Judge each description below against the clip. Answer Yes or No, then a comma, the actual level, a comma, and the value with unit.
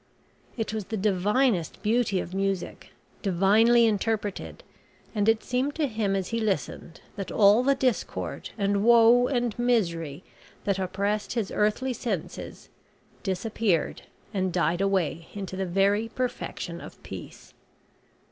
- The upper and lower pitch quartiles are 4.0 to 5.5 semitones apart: No, average, 3.3 semitones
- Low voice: No, high, 205 Hz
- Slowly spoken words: Yes, slow, 130 wpm